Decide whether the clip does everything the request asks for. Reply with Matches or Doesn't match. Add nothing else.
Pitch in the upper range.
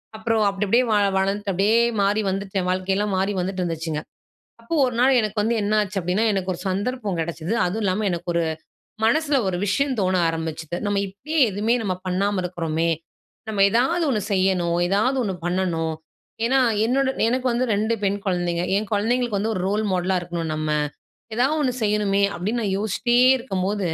Matches